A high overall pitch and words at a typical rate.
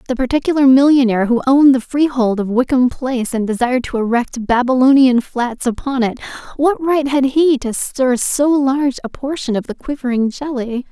Yes: very high, 255 Hz; average, 170 wpm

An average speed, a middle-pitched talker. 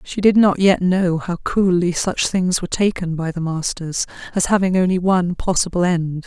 Yes: average, 190 wpm; medium, 180 Hz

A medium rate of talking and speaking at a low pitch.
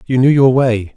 No: fast, 250 wpm; low, 125 Hz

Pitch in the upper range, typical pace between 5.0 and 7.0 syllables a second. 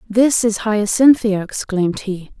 No: high, 215 Hz; 4.2 syllables/s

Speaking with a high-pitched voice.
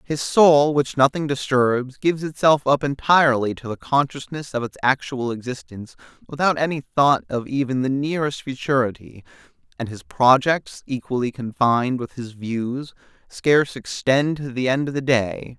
No: low, 135 Hz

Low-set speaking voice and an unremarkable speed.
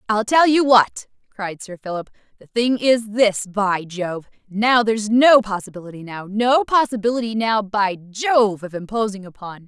No: high, 215 Hz; average, 160 wpm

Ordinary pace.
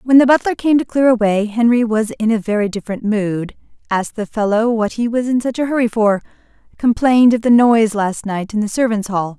No: fast, 215 wpm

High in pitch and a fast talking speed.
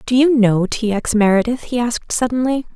No: high, 235 Hz; average, 195 wpm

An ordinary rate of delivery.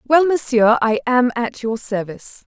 Yes: average, 165 wpm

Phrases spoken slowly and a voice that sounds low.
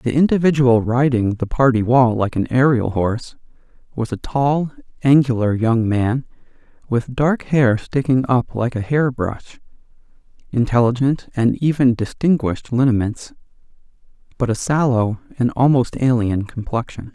Yes: slow, 130 wpm; low, 125 Hz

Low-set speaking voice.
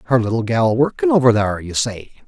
Yes: low, 110 Hz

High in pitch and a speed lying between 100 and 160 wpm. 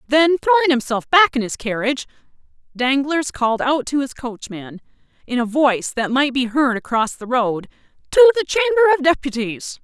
No: very high, 270 Hz; average, 170 wpm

